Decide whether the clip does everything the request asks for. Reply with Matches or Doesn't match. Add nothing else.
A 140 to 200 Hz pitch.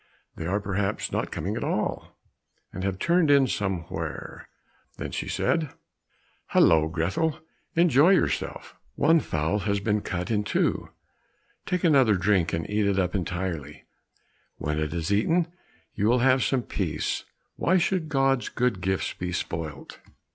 Doesn't match